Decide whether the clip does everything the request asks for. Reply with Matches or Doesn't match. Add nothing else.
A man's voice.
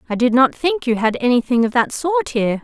Doesn't match